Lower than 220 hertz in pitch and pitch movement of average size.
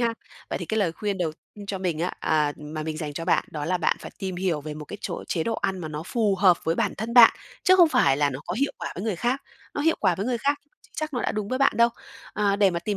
No: high, 190 Hz; wide, 6.2 semitones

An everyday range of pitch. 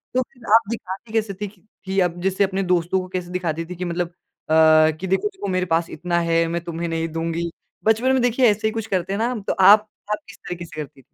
Yes: average, 4.2 semitones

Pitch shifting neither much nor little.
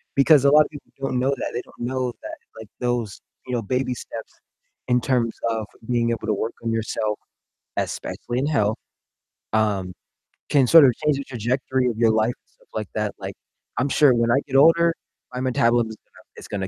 Yes: average, 3.1 semitones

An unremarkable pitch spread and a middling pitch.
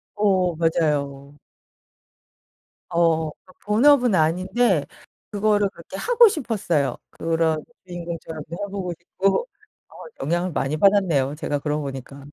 Yes: average, 4.7 semitones; medium, 170 Hz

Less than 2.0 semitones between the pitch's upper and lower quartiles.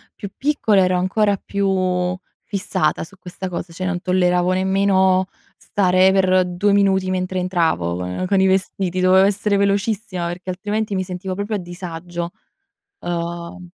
Yes: narrow, 1.6 semitones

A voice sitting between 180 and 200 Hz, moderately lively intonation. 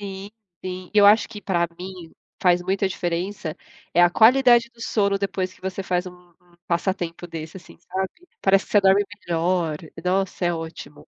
No: medium, 185 Hz; narrow, 2.2 semitones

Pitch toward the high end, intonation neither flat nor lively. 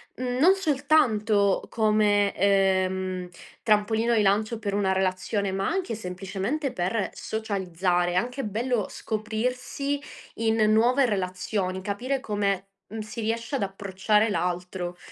Yes: high, 210 Hz; average, 3.3 semitones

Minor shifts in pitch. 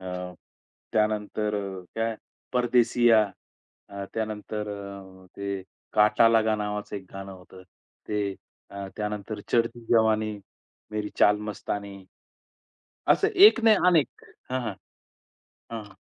Yes: narrow, 2.1 semitones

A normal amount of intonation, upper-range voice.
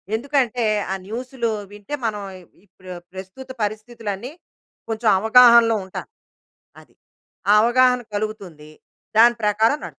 Yes: average, 3.0 semitones; high, 225 Hz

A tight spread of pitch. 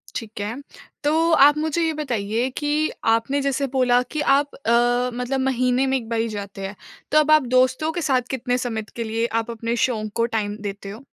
No: average, 4.0 semitones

